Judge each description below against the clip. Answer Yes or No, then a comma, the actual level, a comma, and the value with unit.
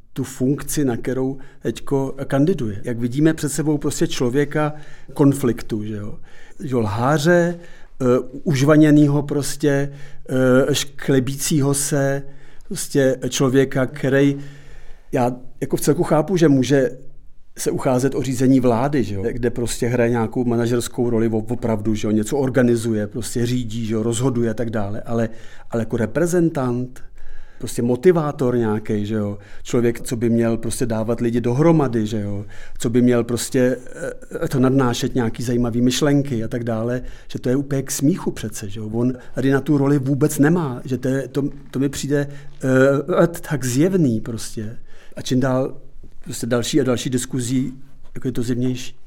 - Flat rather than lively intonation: No, average, 3.1 semitones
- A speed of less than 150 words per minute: No, average, 155 wpm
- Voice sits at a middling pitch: No, low, 130 Hz